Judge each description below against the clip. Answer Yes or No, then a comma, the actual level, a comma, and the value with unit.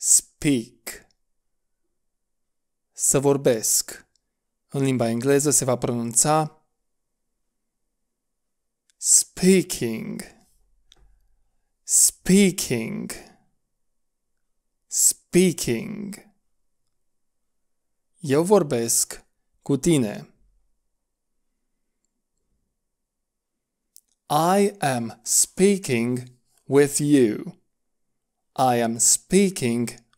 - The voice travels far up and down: Yes, wide, 7.0 semitones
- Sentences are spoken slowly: Yes, slow, 50 wpm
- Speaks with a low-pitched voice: No, medium, 145 Hz